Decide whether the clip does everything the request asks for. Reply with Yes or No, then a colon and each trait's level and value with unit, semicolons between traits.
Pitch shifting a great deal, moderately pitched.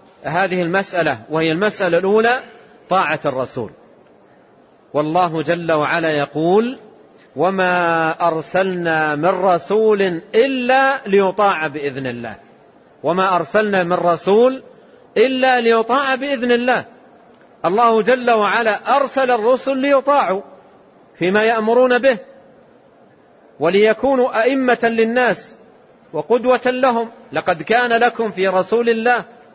No: wide, 5.9 semitones; high, 215 Hz